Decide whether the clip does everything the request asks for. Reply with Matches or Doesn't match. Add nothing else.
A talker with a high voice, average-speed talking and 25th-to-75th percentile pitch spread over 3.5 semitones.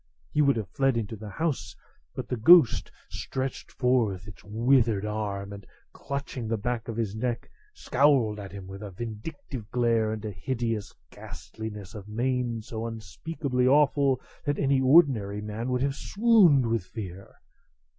Doesn't match